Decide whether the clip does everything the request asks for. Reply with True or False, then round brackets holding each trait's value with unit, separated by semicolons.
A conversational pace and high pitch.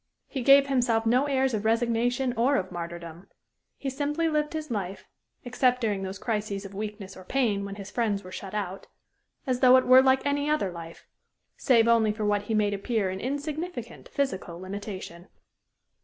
True (180 wpm; 225 Hz)